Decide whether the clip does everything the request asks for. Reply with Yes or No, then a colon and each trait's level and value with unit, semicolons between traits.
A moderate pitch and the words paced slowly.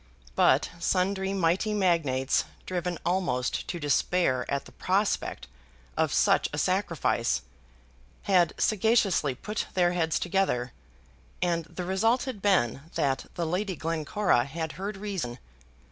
Yes: medium, 180 Hz; slow, 125 wpm